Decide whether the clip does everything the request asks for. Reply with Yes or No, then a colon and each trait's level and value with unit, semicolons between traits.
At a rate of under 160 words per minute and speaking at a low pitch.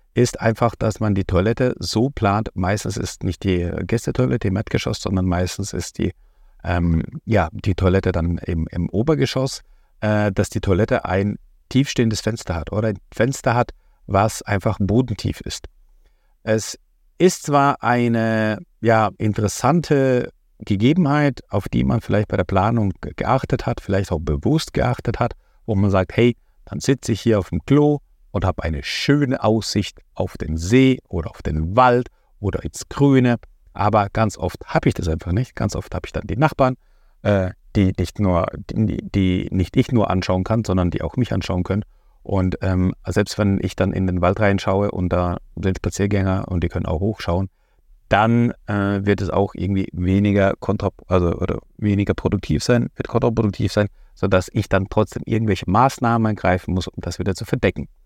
No: average, 175 wpm; low, 100 Hz